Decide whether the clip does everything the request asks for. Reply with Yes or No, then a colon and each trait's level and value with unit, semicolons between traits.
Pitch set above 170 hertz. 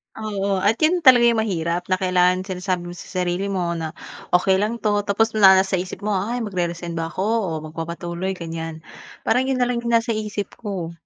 Yes: high, 190 Hz